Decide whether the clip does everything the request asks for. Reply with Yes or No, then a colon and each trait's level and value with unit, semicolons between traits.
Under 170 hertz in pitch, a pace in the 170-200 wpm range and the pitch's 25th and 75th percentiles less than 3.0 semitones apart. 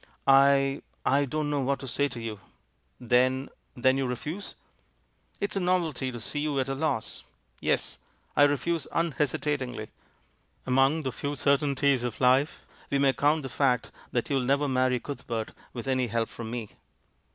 Yes: low, 135 Hz; average, 175 wpm; narrow, 2.6 semitones